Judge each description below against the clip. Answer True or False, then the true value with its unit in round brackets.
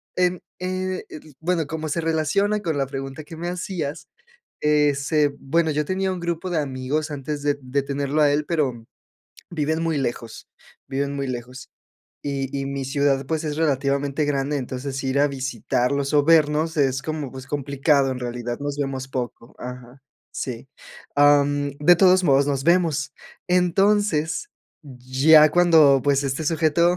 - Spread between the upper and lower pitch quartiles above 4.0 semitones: False (2.9 semitones)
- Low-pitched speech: False (145 Hz)